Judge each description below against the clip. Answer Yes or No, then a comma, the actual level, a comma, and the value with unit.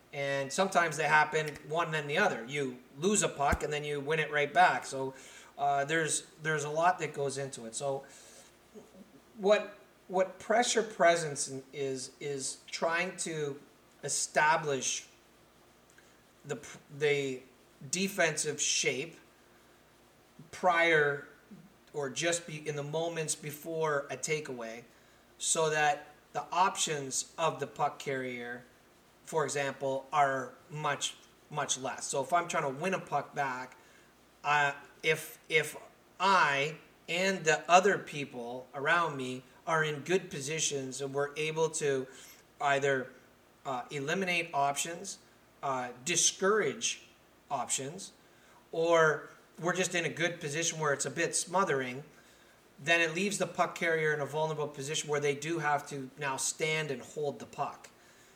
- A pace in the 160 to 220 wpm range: No, average, 140 wpm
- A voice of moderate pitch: Yes, medium, 150 Hz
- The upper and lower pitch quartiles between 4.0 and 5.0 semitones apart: No, average, 3.3 semitones